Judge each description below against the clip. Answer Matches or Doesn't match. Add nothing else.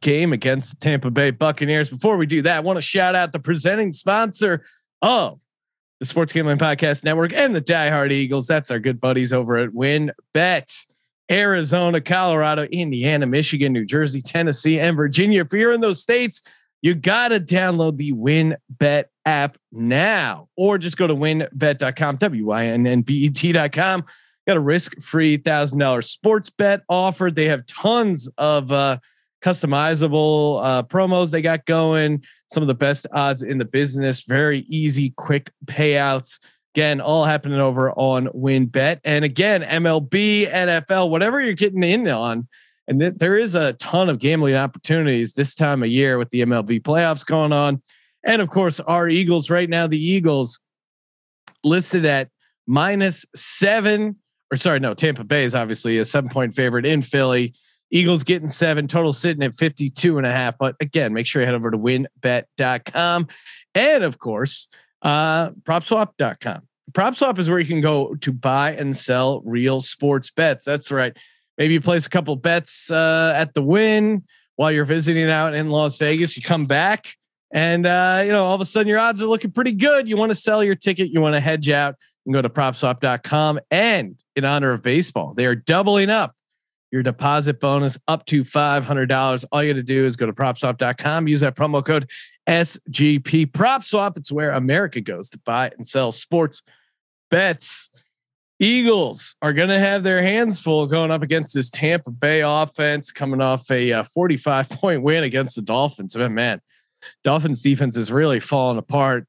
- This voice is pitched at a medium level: Matches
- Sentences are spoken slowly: Doesn't match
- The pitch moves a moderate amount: Matches